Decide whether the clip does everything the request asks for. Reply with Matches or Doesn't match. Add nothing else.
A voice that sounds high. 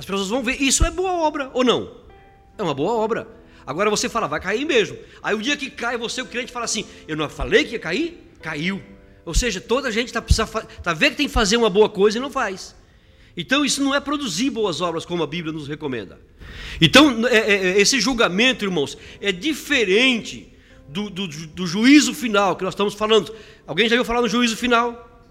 Matches